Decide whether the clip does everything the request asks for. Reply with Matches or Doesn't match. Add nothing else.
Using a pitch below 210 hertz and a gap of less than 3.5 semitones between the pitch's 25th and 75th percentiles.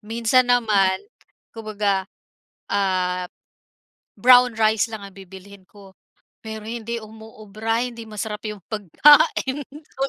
Doesn't match